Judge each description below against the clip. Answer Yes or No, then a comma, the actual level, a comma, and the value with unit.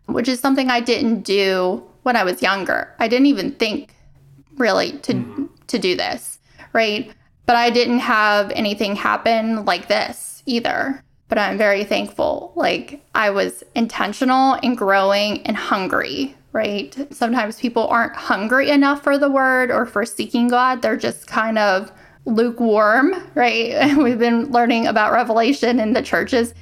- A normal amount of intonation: Yes, average, 3.5 semitones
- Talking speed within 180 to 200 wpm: No, average, 155 wpm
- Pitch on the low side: No, high, 235 Hz